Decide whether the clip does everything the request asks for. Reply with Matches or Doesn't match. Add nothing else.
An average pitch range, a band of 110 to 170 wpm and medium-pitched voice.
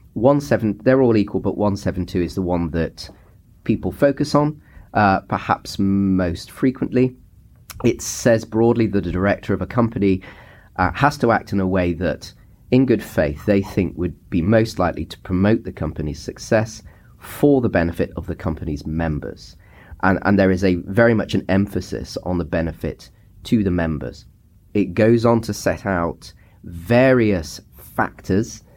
Doesn't match